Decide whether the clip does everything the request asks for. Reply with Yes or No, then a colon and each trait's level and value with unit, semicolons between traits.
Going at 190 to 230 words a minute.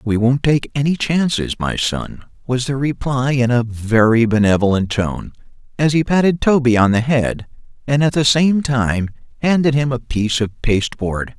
No: average, 175 wpm